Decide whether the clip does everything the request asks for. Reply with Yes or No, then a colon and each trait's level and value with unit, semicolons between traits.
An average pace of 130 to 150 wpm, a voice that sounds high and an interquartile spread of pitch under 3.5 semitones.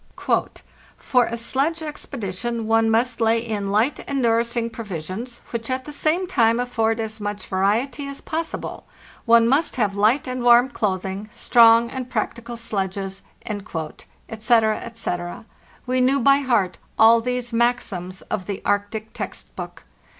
Yes: average, 145 wpm; high, 230 Hz; average, 2.8 semitones